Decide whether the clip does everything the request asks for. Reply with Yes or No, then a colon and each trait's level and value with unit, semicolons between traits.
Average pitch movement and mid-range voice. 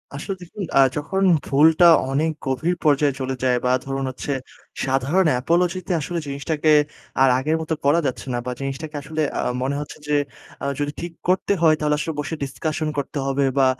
Yes: average, 3.0 semitones; medium, 150 Hz